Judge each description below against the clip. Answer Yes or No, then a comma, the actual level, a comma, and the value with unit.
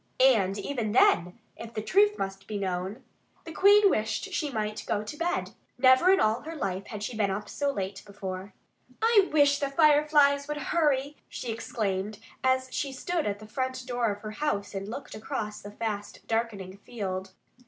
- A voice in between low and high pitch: No, high, 230 Hz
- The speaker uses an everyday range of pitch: No, wide, 5.9 semitones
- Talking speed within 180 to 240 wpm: Yes, average, 185 wpm